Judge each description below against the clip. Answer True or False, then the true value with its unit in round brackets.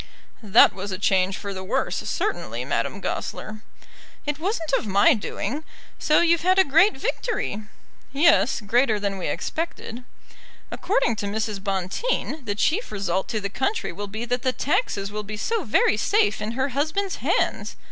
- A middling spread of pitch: False (7.9 semitones)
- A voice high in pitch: True (230 Hz)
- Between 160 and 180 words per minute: True (165 wpm)